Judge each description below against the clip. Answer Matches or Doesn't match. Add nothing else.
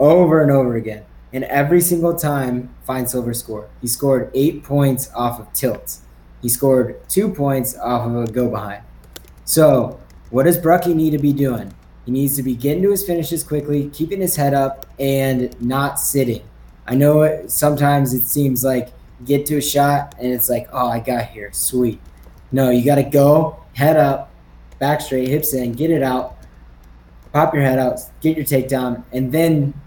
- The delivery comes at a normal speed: Matches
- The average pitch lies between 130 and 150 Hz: Matches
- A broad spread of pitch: Doesn't match